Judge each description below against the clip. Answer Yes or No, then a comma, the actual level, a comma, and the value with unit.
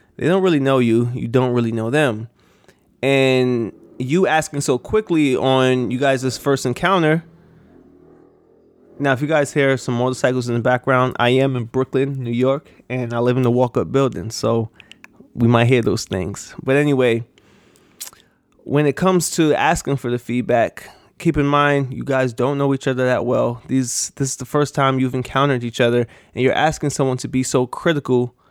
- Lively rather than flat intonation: No, narrow, 2.6 semitones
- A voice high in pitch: No, low, 130 Hz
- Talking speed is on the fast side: No, average, 185 wpm